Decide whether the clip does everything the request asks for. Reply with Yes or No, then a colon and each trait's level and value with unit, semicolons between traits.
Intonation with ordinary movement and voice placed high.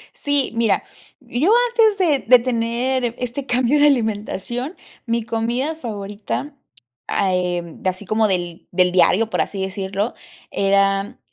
Yes: average, 4.7 semitones; high, 225 Hz